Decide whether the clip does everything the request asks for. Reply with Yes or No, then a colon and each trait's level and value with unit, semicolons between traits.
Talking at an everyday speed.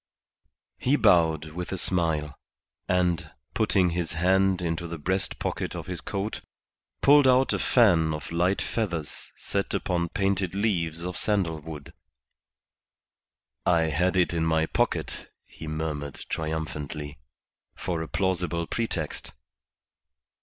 No: slow, 125 wpm